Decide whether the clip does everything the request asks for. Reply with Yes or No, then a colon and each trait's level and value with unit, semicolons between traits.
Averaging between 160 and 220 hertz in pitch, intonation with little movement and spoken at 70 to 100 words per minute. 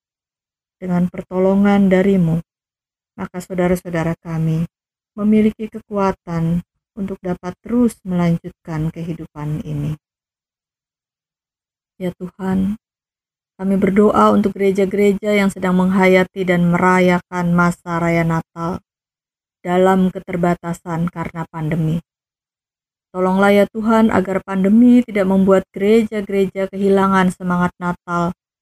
Yes: medium, 185 Hz; narrow, 2.3 semitones; average, 90 wpm